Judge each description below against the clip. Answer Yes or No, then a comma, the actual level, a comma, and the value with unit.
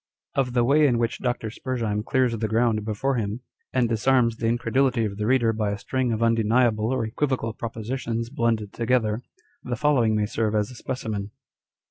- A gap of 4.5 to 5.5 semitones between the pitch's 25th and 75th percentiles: No, narrow, 2.6 semitones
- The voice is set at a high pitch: No, low, 115 Hz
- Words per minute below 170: No, average, 180 wpm